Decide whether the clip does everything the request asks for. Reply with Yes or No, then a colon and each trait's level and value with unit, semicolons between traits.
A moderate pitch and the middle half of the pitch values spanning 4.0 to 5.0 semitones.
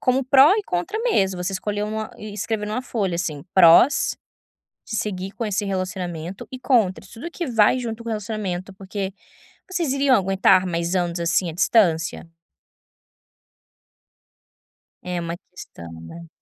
No: high, 195 Hz; average, 4.3 semitones